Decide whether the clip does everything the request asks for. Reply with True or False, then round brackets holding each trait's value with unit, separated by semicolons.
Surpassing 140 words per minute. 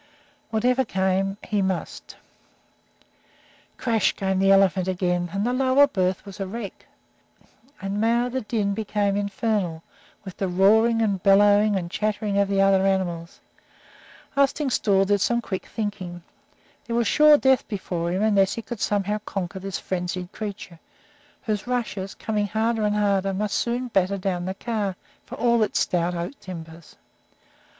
True (150 wpm)